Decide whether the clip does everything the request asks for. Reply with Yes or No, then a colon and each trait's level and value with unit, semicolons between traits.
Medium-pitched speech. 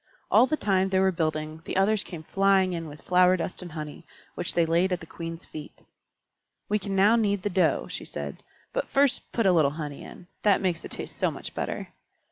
Yes: medium, 180 Hz